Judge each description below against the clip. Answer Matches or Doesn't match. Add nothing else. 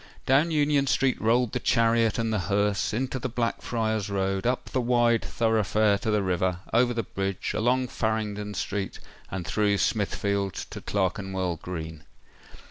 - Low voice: Matches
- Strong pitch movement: Doesn't match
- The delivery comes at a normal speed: Doesn't match